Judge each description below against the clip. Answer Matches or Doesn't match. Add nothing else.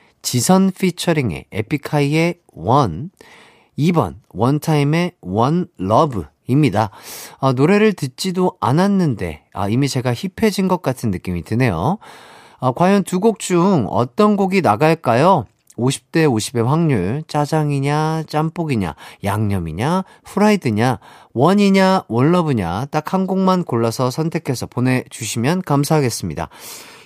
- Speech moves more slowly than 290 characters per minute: Matches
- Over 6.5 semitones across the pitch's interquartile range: Matches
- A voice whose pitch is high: Doesn't match